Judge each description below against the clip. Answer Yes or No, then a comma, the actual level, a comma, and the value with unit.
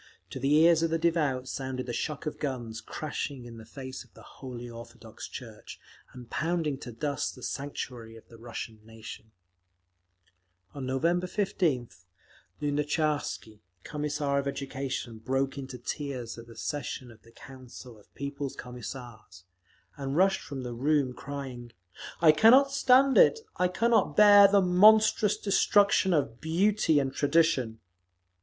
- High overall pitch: No, medium, 140 Hz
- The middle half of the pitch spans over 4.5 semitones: Yes, average, 5.1 semitones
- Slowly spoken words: No, average, 145 wpm